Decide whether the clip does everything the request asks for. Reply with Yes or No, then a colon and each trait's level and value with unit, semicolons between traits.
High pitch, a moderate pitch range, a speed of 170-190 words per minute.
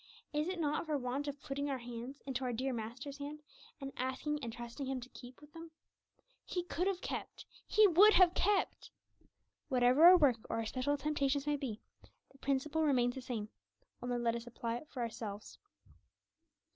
Yes: very high, 270 Hz; average, 3.5 semitones; average, 185 wpm